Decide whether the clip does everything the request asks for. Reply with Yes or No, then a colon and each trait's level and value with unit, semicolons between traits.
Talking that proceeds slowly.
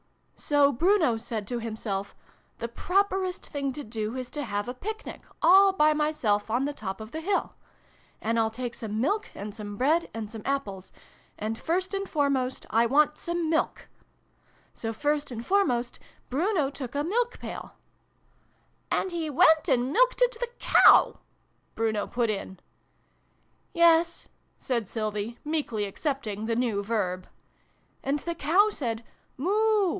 No: average, 165 wpm